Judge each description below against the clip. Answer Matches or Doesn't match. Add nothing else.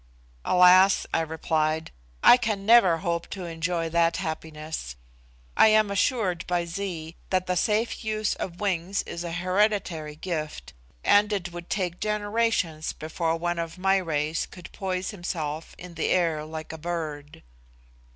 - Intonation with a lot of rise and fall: Doesn't match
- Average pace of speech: Matches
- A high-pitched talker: Doesn't match